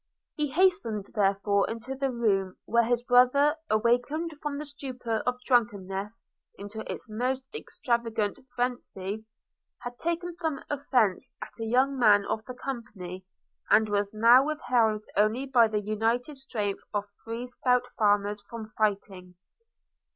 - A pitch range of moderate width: Yes, average, 3.7 semitones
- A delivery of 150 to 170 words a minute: No, slow, 135 wpm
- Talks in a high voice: Yes, high, 235 Hz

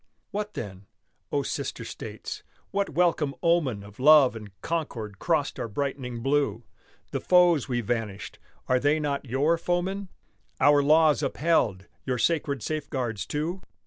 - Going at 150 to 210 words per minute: No, average, 140 wpm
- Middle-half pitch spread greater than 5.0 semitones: Yes, wide, 5.6 semitones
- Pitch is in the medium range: Yes, medium, 145 Hz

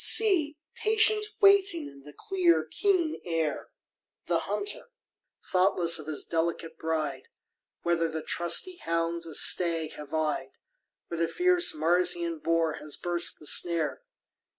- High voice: No, medium, 170 Hz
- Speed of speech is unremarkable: No, slow, 130 wpm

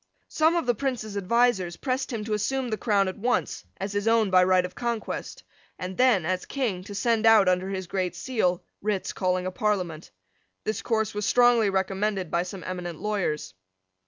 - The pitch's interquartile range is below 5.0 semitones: Yes, average, 3.8 semitones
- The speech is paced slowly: No, average, 190 wpm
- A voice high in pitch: Yes, high, 205 Hz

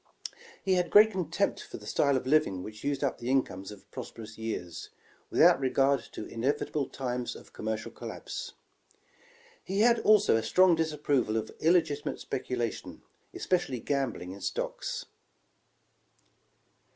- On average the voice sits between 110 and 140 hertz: Yes, low, 135 Hz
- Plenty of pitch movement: Yes, wide, 6.2 semitones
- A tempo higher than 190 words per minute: No, slow, 135 wpm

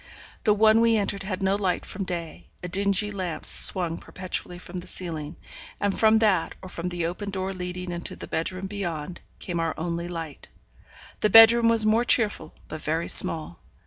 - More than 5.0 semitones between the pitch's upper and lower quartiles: No, average, 3.2 semitones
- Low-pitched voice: No, medium, 185 Hz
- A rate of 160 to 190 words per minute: Yes, average, 180 wpm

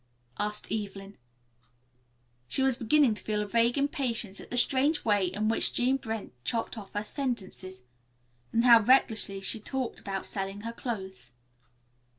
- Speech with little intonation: No, average, 3.8 semitones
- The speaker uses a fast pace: No, average, 155 wpm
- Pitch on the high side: Yes, high, 220 Hz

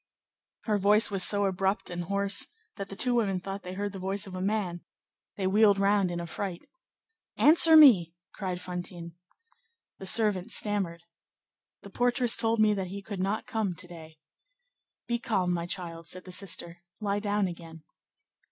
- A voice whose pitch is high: Yes, high, 195 Hz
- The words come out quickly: No, average, 170 wpm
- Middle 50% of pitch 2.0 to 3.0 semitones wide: Yes, narrow, 2.6 semitones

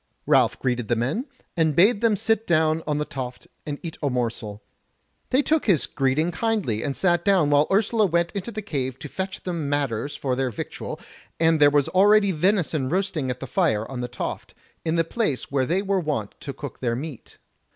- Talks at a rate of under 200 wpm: No, fast, 205 wpm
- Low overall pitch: No, medium, 155 Hz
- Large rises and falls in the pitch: Yes, wide, 6.4 semitones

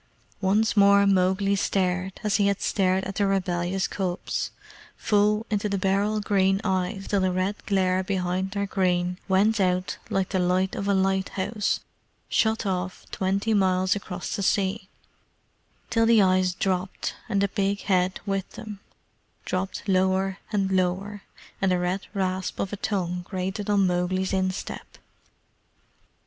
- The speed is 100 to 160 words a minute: Yes, average, 150 wpm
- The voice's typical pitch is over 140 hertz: Yes, high, 190 Hz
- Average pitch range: No, narrow, 1.4 semitones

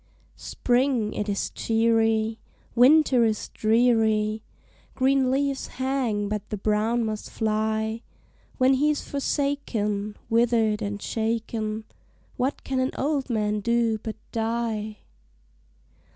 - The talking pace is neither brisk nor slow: No, slow, 110 wpm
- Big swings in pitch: No, average, 3.0 semitones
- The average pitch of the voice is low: No, high, 225 Hz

